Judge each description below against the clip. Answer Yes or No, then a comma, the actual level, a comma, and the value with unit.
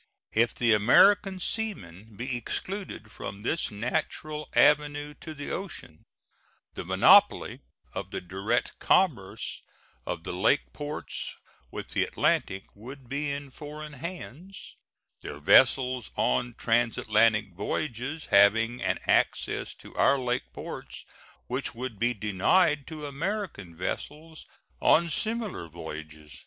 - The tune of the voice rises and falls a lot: Yes, wide, 6.4 semitones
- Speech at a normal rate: No, slow, 120 wpm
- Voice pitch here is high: No, low, 125 Hz